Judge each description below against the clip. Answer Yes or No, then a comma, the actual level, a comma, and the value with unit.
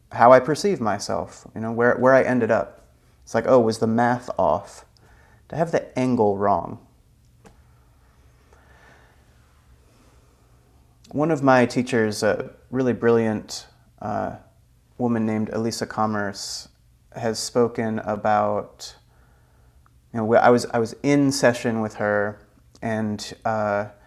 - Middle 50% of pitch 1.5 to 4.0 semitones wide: Yes, average, 3.7 semitones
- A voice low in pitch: Yes, low, 110 Hz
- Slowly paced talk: Yes, slow, 125 wpm